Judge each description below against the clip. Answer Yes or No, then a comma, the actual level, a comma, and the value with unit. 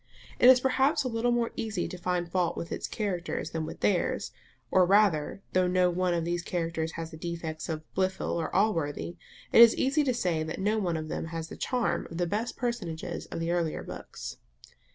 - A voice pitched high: No, medium, 180 Hz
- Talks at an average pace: No, fast, 215 wpm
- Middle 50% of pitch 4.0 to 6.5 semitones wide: Yes, average, 4.6 semitones